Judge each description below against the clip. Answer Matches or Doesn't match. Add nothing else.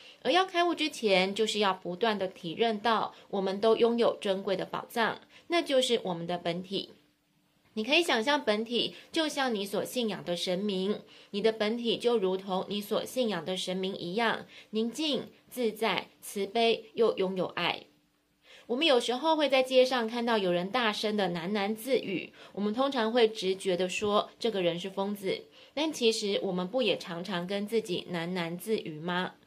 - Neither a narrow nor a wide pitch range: Matches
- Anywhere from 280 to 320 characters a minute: Doesn't match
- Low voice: Doesn't match